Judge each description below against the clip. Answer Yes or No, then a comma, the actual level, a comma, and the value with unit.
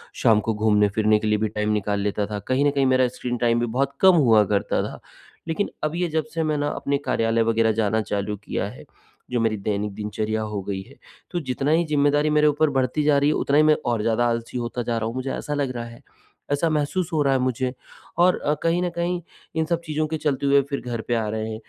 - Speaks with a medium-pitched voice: No, low, 125 Hz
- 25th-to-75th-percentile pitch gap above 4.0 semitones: Yes, average, 5.3 semitones